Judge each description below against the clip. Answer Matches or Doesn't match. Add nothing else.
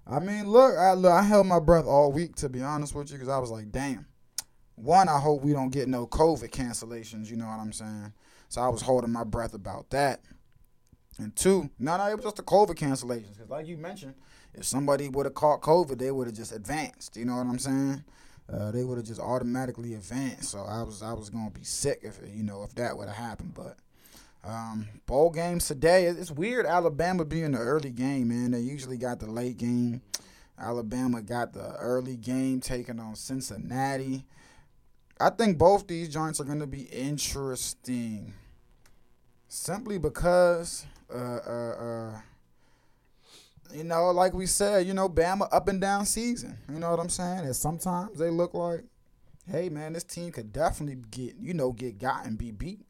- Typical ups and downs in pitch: Doesn't match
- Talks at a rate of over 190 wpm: Matches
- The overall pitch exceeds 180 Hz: Doesn't match